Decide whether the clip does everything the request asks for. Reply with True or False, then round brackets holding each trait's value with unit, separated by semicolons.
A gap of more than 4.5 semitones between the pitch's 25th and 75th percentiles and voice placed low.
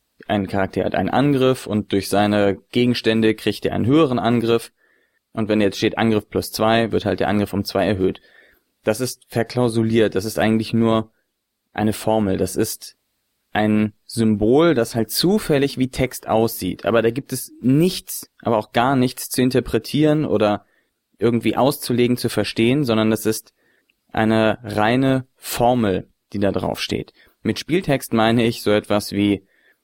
False (2.8 semitones; 110 Hz)